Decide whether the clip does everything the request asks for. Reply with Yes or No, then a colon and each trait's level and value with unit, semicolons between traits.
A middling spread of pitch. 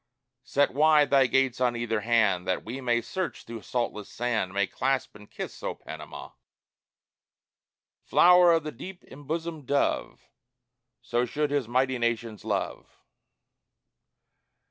Yes: average, 3.8 semitones